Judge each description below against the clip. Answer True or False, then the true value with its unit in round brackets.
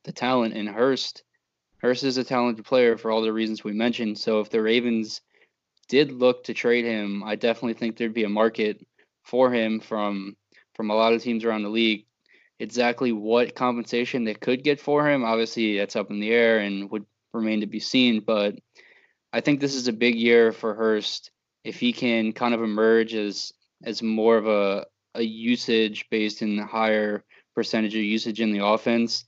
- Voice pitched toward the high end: False (115 Hz)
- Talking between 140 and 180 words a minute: False (195 wpm)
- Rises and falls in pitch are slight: True (1.8 semitones)